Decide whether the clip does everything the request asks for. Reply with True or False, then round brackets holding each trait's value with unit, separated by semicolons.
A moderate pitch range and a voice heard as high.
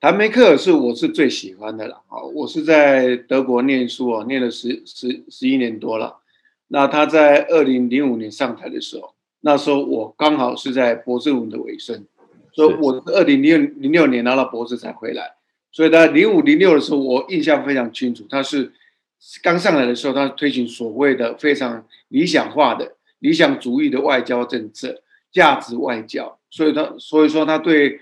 False (4.8 semitones; 140 Hz)